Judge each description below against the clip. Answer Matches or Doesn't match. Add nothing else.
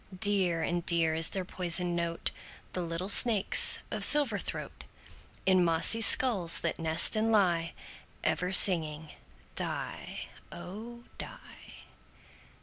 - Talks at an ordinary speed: Doesn't match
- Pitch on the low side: Doesn't match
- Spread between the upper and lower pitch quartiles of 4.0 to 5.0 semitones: Doesn't match